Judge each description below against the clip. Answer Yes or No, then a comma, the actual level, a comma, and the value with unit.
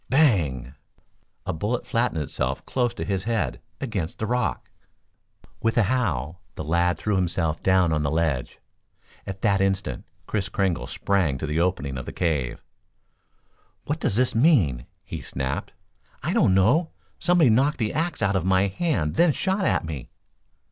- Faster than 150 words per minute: Yes, average, 160 wpm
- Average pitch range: No, wide, 7.1 semitones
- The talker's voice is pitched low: Yes, very low, 95 Hz